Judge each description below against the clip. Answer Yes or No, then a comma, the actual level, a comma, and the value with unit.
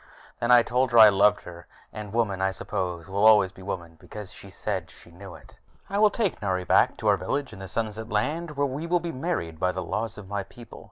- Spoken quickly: Yes, fast, 240 wpm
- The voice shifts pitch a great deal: No, average, 4.6 semitones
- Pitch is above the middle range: No, low, 105 Hz